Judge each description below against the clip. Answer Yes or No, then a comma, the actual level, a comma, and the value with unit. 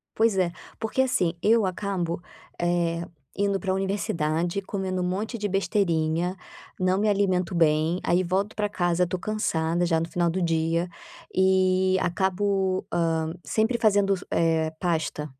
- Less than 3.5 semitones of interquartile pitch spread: Yes, average, 2.8 semitones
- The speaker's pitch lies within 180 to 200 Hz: Yes, medium, 185 Hz